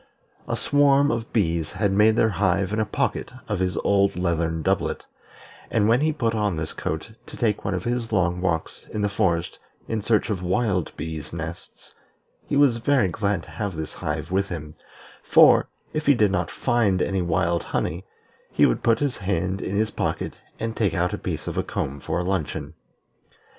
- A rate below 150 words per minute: No, average, 195 wpm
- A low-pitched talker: Yes, very low, 95 Hz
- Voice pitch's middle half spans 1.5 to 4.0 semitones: No, average, 4.7 semitones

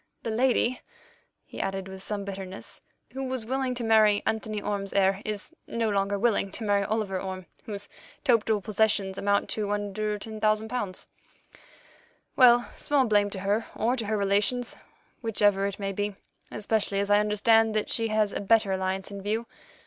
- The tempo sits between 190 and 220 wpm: No, average, 165 wpm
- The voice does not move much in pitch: Yes, narrow, 2.0 semitones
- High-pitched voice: Yes, high, 210 Hz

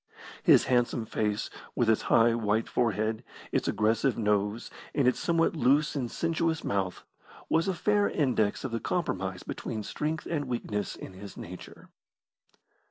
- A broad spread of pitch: Yes, wide, 6.1 semitones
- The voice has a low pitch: Yes, low, 115 Hz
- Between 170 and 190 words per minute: No, average, 150 wpm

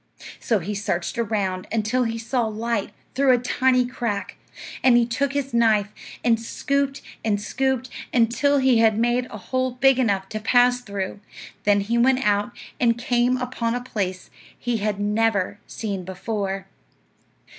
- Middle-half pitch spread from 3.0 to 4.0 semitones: Yes, average, 3.3 semitones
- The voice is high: Yes, high, 230 Hz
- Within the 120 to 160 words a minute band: Yes, average, 155 wpm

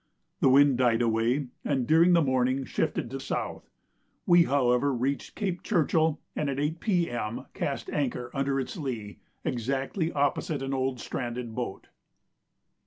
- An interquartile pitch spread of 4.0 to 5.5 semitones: No, average, 3.2 semitones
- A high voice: No, low, 135 Hz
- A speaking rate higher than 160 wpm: No, average, 145 wpm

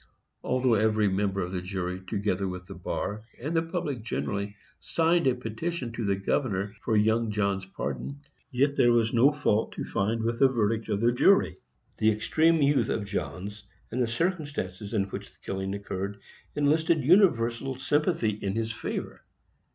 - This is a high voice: No, low, 110 Hz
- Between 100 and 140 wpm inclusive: No, average, 170 wpm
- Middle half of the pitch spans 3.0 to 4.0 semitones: No, average, 5.2 semitones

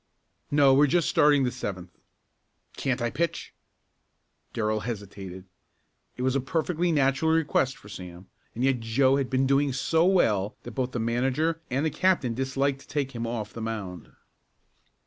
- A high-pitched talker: No, low, 130 Hz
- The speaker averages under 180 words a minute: Yes, average, 165 wpm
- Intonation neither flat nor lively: Yes, average, 4.0 semitones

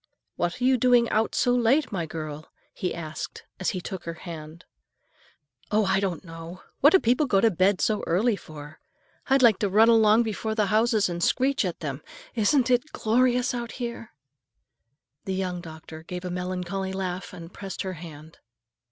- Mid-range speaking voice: No, high, 195 Hz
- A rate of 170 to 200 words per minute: Yes, average, 180 wpm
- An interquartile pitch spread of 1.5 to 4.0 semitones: No, average, 5.3 semitones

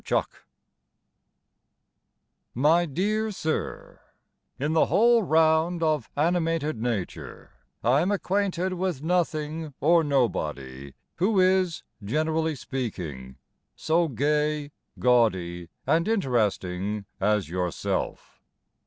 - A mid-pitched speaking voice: Yes, medium, 150 Hz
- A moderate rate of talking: No, slow, 100 wpm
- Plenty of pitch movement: Yes, wide, 7.5 semitones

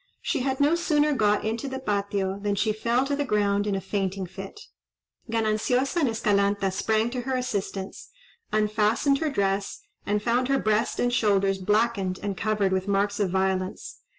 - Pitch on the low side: No, high, 210 Hz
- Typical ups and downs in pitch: Yes, average, 3.7 semitones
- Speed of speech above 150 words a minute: Yes, average, 175 wpm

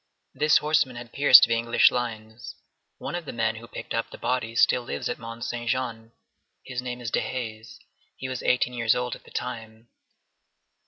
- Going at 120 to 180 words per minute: No, average, 190 wpm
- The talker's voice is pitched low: Yes, low, 120 Hz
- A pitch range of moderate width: No, narrow, 1.7 semitones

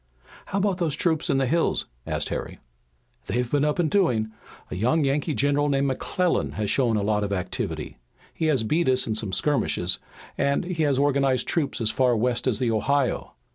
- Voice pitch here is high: No, low, 135 Hz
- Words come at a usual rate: Yes, average, 195 wpm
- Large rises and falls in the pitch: No, average, 4.6 semitones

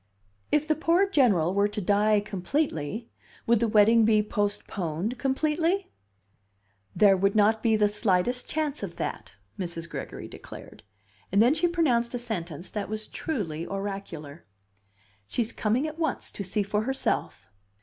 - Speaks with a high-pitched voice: Yes, high, 215 Hz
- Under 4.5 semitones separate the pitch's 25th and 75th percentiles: No, average, 4.8 semitones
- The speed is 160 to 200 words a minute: No, average, 150 wpm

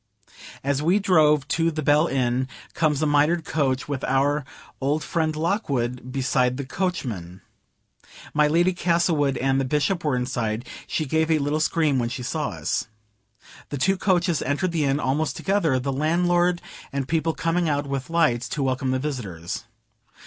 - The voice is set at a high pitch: No, medium, 145 Hz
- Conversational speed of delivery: Yes, average, 165 wpm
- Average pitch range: Yes, average, 3.9 semitones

